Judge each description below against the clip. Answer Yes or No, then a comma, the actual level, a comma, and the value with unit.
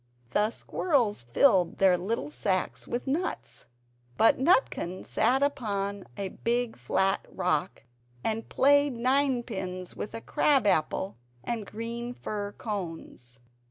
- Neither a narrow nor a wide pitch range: Yes, average, 4.7 semitones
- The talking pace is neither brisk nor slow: No, slow, 120 wpm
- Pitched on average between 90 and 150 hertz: No, high, 215 Hz